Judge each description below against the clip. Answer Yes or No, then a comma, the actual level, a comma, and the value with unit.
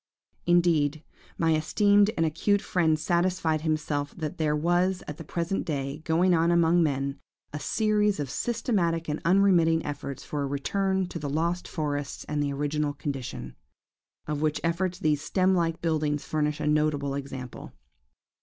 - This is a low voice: No, medium, 160 Hz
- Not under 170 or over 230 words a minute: No, average, 155 wpm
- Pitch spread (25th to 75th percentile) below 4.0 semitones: Yes, average, 3.0 semitones